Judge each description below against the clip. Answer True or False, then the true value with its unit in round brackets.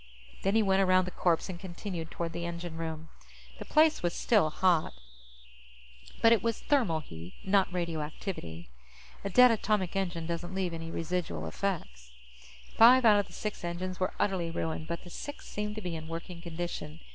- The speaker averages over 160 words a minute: True (180 wpm)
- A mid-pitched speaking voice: True (175 Hz)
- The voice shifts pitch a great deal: False (3.2 semitones)